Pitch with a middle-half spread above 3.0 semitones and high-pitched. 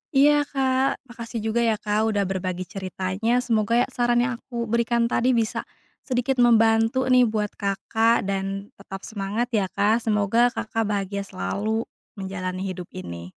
Yes: average, 3.4 semitones; high, 220 Hz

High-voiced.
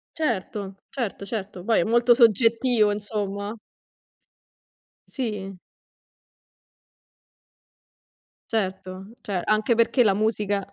Yes: high, 210 Hz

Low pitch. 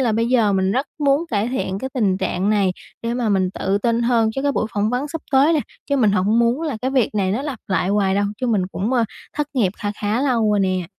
No: high, 225 Hz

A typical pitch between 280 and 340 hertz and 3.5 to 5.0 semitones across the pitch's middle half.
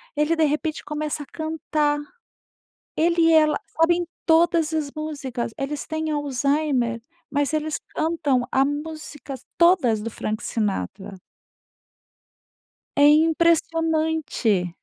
No: very high, 300 Hz; average, 2.8 semitones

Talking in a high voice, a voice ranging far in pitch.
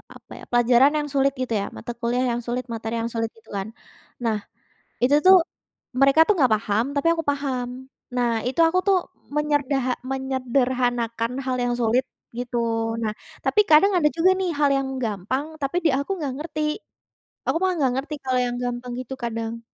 No: very high, 255 Hz; average, 3.4 semitones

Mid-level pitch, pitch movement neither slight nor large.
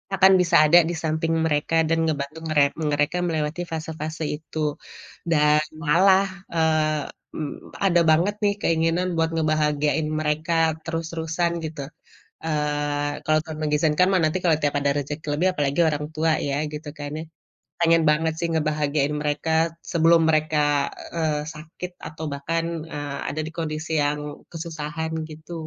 No: medium, 155 Hz; narrow, 1.6 semitones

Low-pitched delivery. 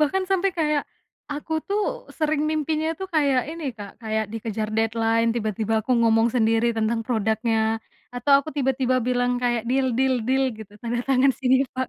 No: high, 245 Hz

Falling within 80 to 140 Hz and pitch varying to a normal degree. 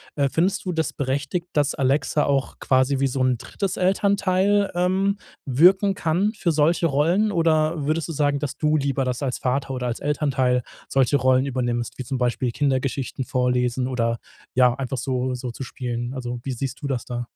Yes: low, 135 Hz; average, 4.2 semitones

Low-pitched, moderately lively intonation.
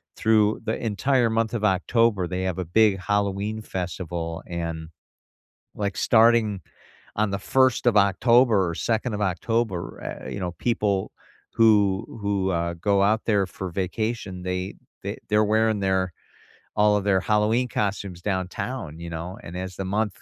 Yes: low, 100 Hz; average, 3.1 semitones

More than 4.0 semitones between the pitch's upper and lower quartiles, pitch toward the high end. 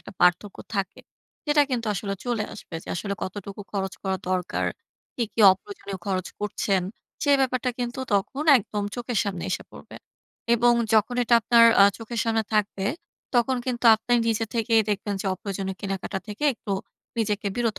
No: average, 3.3 semitones; high, 210 Hz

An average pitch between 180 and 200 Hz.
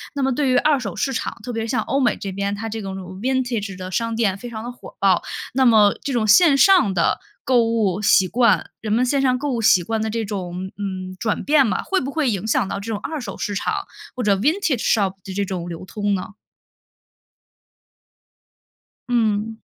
No: high, 220 Hz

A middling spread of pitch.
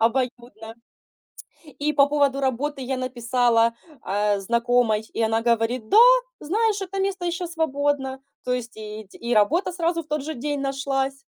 Yes: average, 4.2 semitones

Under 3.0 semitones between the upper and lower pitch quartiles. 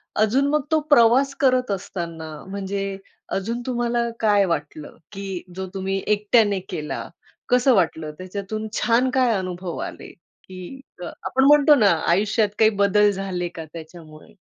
No: average, 4.4 semitones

